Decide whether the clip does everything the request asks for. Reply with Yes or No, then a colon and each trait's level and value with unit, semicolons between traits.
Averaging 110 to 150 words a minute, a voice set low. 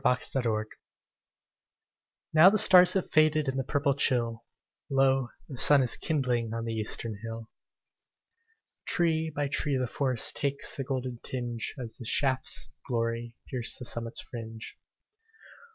Yes: average, 145 wpm; low, 130 Hz